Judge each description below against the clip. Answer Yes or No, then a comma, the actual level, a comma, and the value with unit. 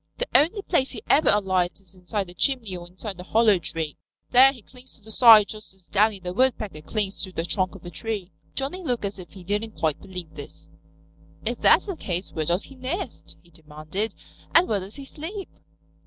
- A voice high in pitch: Yes, high, 205 Hz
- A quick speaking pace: Yes, fast, 215 wpm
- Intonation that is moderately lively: No, wide, 5.8 semitones